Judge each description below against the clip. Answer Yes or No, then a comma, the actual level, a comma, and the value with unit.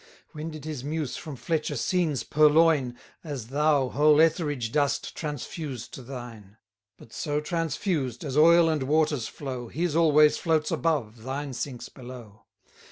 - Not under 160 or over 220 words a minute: No, average, 145 wpm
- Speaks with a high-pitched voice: No, medium, 145 Hz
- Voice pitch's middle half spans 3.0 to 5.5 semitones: Yes, average, 3.5 semitones